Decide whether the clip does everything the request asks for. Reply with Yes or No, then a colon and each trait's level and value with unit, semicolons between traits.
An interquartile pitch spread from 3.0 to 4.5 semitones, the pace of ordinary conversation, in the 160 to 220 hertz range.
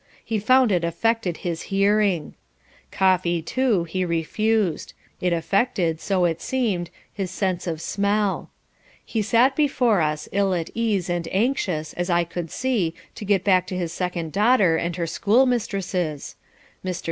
Yes: average, 3.9 semitones; average, 150 wpm; medium, 185 Hz